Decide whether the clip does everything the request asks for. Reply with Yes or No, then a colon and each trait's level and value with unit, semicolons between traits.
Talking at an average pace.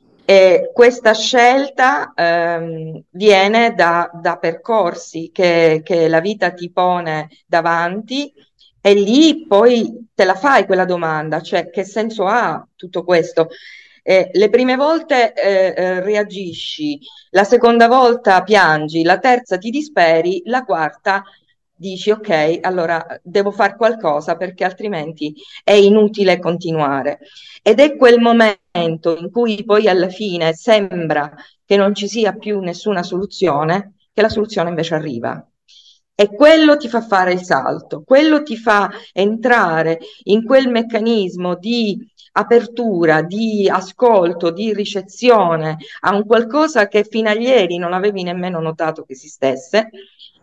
Yes: average, 130 wpm